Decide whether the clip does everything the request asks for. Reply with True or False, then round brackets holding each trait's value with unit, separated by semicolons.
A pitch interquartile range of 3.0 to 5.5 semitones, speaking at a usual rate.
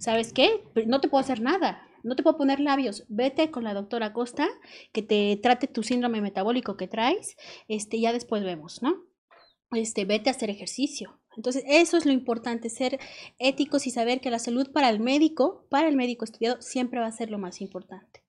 False (3.6 semitones; 200 wpm)